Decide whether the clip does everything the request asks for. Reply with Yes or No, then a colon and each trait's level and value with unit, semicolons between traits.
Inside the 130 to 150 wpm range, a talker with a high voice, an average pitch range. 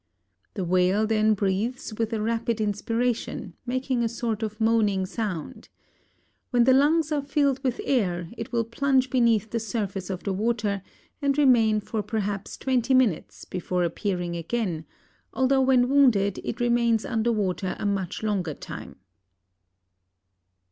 Yes: average, 145 wpm; high, 225 Hz; average, 3.7 semitones